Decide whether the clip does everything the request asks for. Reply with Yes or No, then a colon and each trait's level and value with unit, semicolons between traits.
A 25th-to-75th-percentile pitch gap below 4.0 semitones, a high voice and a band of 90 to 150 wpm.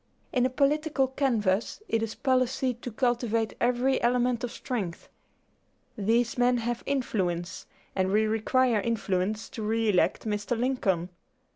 Yes: average, 3.1 semitones; high, 235 Hz; slow, 135 wpm